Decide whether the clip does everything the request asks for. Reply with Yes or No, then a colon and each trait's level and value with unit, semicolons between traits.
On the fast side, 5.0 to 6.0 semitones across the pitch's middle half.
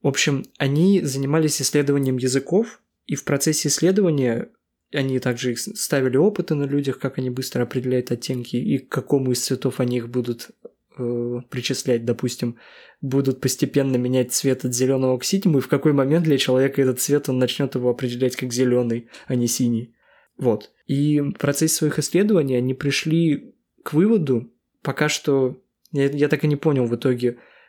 No: fast, 165 wpm; average, 2.7 semitones